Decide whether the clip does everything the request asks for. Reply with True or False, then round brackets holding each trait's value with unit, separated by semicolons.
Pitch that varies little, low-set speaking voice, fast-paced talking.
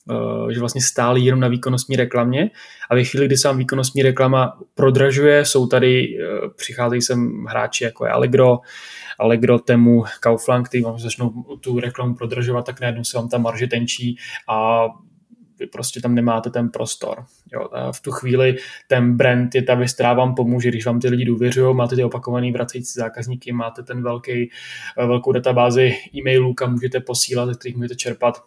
True (1.1 semitones; 125 Hz; 175 wpm)